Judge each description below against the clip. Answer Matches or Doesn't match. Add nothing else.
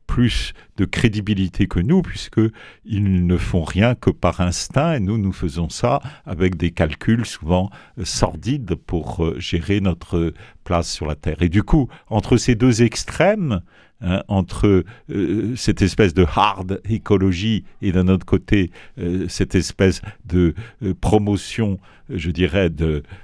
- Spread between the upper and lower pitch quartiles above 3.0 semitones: Matches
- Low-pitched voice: Matches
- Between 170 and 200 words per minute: Doesn't match